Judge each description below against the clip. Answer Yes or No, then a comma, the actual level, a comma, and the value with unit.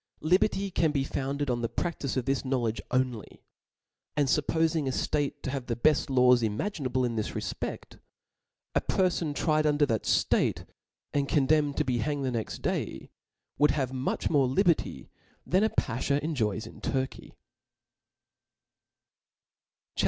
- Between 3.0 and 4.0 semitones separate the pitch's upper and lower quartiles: Yes, average, 3.3 semitones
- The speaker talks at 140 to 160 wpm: Yes, average, 150 wpm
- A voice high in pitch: No, low, 135 Hz